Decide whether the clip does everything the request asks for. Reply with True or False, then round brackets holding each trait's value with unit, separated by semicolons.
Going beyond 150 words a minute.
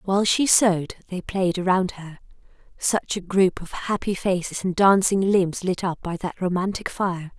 True (180 wpm)